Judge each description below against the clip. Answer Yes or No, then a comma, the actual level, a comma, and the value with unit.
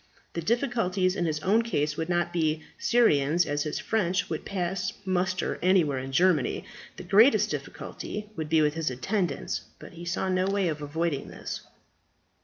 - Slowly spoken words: No, average, 170 wpm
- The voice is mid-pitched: Yes, medium, 175 Hz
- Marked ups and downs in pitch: No, average, 3.7 semitones